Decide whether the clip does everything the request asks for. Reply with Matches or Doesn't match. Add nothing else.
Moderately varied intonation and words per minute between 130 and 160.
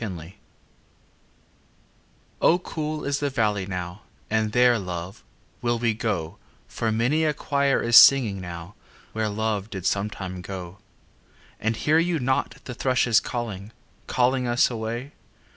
Matches